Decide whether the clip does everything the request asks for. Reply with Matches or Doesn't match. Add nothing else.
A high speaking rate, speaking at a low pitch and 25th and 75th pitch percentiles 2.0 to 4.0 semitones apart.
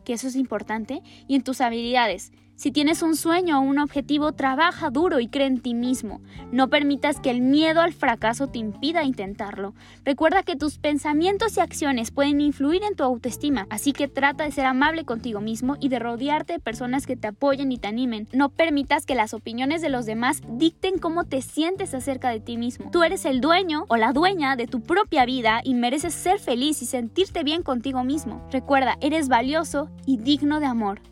Doesn't match